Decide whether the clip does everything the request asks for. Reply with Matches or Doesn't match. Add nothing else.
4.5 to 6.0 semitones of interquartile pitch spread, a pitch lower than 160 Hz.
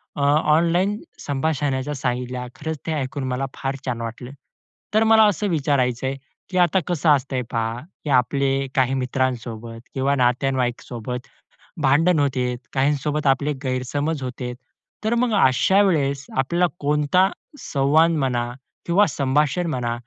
Doesn't match